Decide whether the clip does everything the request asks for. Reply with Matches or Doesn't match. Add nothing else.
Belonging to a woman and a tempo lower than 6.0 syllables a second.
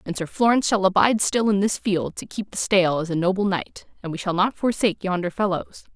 Doesn't match